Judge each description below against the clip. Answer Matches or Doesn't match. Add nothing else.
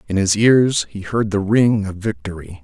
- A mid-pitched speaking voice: Doesn't match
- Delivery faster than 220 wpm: Doesn't match